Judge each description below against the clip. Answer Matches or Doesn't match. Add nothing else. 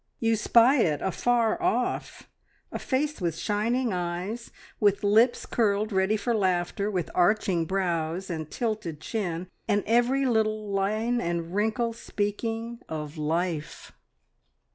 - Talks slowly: Matches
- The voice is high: Matches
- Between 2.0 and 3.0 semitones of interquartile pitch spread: Doesn't match